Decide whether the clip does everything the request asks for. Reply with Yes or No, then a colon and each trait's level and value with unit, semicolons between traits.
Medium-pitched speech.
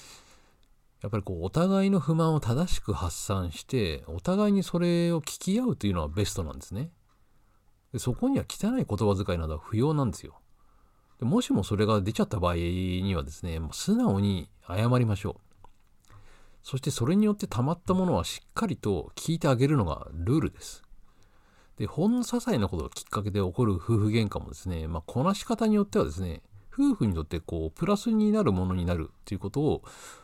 No: low, 105 Hz